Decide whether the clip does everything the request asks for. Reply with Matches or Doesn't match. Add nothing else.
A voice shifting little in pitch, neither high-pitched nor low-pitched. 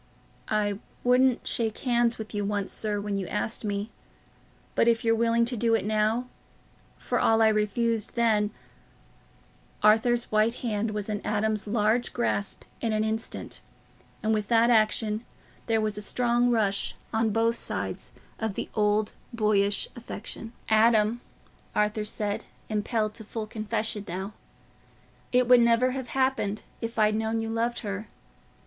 Doesn't match